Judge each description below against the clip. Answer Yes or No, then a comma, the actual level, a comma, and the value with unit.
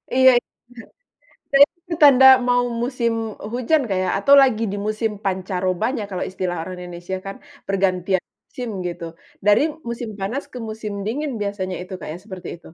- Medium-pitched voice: No, high, 205 Hz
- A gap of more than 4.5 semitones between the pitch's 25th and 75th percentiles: Yes, average, 4.9 semitones